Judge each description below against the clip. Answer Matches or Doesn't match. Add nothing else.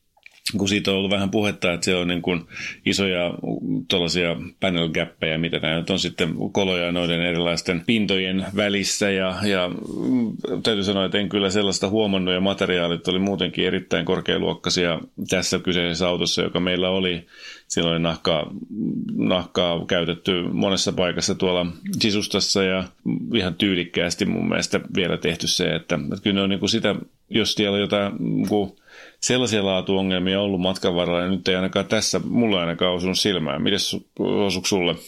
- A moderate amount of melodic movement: Doesn't match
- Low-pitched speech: Matches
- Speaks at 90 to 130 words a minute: Doesn't match